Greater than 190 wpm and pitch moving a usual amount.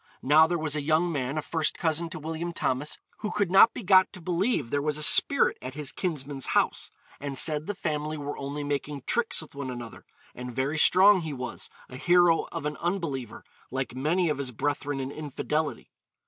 Yes: fast, 205 wpm; average, 3.4 semitones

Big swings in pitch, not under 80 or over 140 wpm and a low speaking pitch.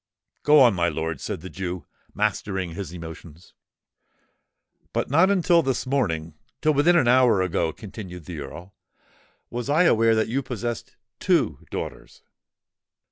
Yes: wide, 7.7 semitones; slow, 135 wpm; low, 105 Hz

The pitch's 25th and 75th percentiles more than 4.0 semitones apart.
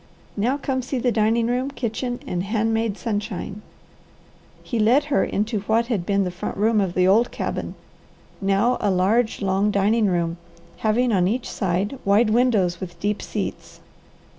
No: average, 3.3 semitones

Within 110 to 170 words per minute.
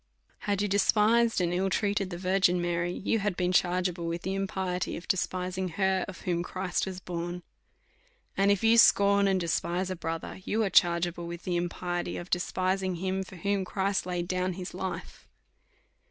No: average, 180 wpm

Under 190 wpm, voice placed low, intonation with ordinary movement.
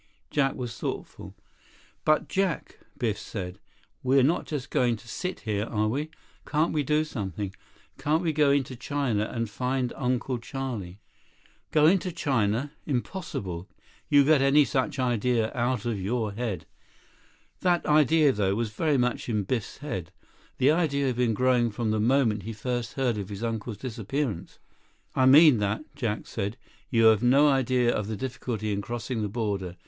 Yes: average, 165 wpm; low, 125 Hz; average, 4.5 semitones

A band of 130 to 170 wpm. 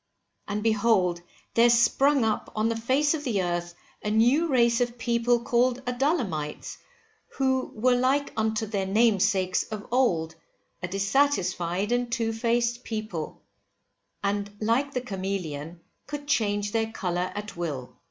Yes: average, 140 wpm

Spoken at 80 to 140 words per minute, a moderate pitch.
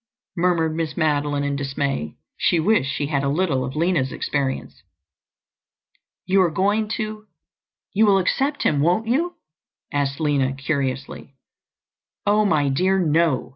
Yes: slow, 135 wpm; medium, 155 Hz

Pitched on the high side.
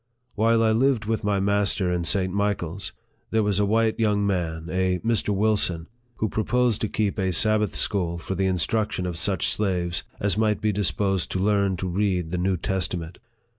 No: low, 100 Hz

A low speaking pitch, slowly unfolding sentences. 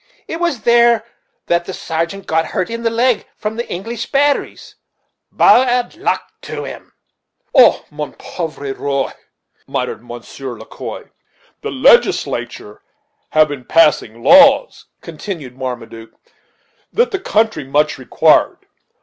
No: medium, 175 Hz; slow, 130 wpm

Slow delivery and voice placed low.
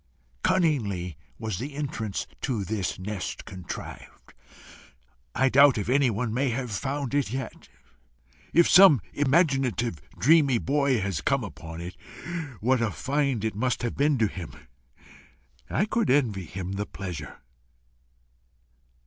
Yes: slow, 130 wpm; low, 120 Hz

